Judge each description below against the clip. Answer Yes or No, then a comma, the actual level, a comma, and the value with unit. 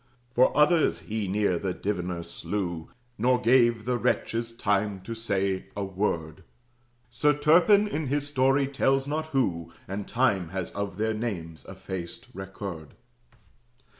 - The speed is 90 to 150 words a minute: Yes, slow, 135 wpm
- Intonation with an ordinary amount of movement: No, wide, 5.7 semitones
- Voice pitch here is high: No, low, 105 Hz